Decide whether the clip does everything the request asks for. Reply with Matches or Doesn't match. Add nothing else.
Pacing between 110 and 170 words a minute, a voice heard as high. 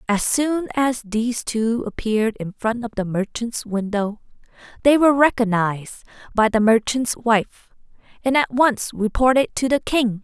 Matches